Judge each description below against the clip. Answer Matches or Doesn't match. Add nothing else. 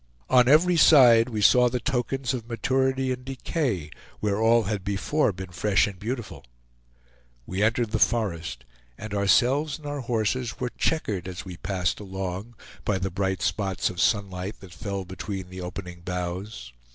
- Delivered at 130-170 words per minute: Matches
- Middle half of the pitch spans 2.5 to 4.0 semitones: Doesn't match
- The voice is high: Doesn't match